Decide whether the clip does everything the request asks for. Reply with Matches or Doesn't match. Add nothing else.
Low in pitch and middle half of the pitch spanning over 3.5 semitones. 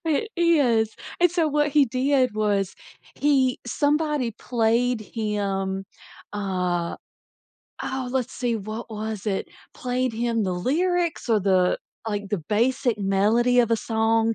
Doesn't match